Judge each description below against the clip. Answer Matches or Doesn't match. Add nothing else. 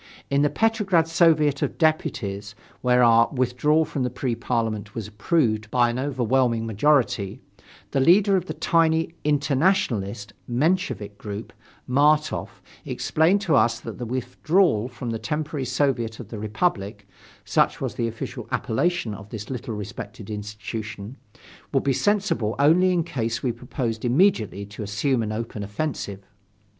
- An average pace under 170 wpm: Matches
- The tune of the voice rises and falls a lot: Matches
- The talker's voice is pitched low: Matches